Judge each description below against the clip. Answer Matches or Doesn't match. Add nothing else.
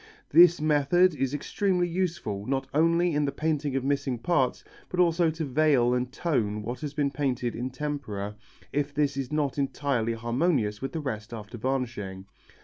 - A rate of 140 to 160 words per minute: Doesn't match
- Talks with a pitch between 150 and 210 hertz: Doesn't match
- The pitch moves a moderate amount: Matches